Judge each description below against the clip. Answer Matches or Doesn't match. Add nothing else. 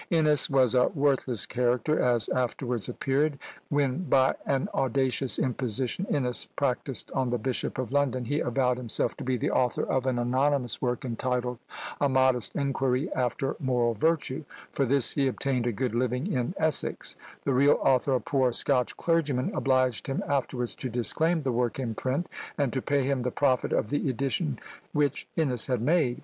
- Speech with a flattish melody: Matches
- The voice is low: Matches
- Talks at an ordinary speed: Matches